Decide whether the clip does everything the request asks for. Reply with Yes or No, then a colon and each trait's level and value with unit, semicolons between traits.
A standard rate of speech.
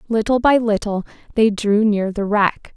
Yes: average, 175 wpm